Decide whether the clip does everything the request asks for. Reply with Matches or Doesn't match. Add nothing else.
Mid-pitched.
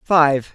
Matches